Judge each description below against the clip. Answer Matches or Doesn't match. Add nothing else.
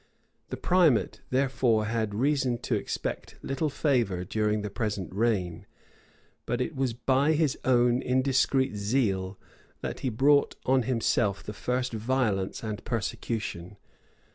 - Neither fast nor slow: Doesn't match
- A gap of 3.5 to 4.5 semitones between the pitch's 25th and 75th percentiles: Matches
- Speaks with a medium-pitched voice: Doesn't match